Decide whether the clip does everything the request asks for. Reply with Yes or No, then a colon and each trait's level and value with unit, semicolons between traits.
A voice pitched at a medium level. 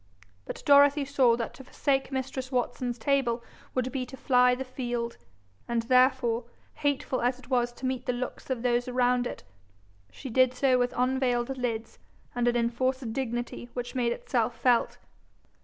No: very high, 250 Hz